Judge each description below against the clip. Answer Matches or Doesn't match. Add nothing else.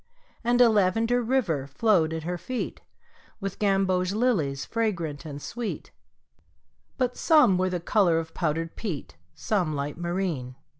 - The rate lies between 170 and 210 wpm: Doesn't match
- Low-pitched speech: Doesn't match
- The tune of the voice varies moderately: Doesn't match